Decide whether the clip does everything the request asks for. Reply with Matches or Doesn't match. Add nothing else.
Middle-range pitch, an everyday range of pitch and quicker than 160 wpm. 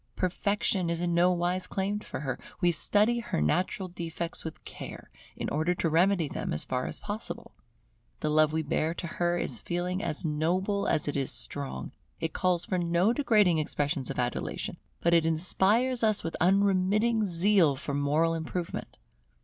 Matches